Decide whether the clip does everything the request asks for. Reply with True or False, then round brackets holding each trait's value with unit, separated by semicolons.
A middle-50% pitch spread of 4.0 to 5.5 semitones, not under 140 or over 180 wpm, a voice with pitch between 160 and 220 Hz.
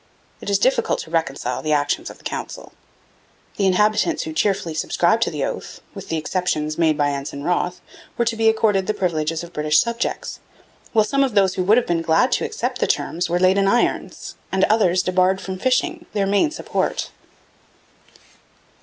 False (4.9 semitones; 195 wpm; 185 Hz)